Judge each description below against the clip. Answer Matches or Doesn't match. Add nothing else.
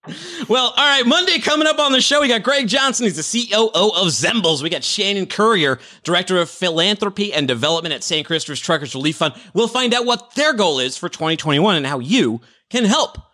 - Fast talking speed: Matches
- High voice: Matches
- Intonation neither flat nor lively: Doesn't match